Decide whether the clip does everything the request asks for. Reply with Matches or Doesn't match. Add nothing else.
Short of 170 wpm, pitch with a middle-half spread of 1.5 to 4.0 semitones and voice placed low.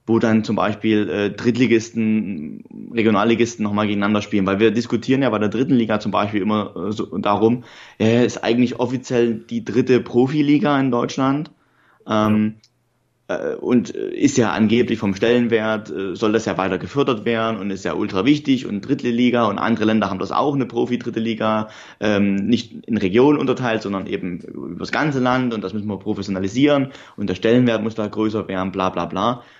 Doesn't match